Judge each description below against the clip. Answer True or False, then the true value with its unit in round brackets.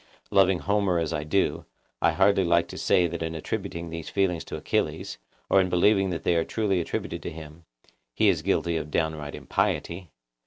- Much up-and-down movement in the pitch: False (2.8 semitones)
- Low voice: True (85 Hz)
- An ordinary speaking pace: True (190 wpm)